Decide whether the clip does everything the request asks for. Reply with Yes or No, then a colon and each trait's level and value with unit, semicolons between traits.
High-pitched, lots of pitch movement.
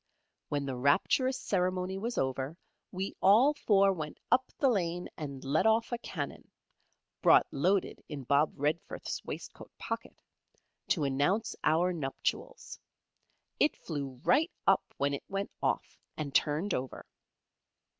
No: medium, 170 Hz; wide, 6.0 semitones